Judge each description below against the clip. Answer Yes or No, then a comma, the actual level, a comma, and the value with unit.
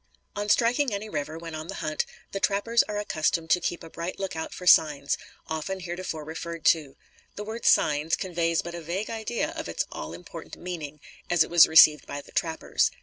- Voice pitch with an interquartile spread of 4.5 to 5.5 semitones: No, average, 3.9 semitones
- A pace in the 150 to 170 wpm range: No, average, 200 wpm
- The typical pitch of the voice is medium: Yes, medium, 170 Hz